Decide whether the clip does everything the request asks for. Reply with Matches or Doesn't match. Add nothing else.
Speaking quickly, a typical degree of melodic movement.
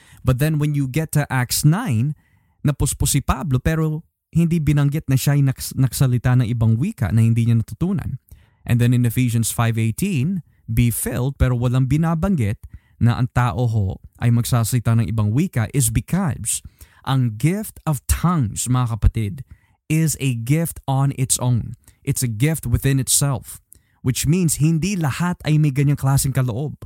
Matches